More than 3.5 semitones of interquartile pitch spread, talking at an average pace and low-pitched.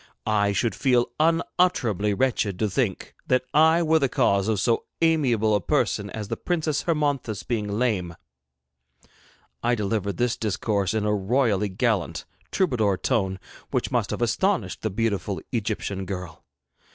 Yes: average, 4.6 semitones; average, 145 wpm; low, 110 Hz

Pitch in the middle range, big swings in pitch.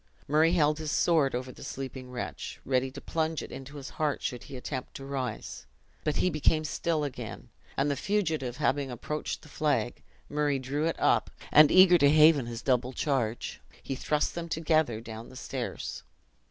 No: medium, 145 Hz; average, 3.3 semitones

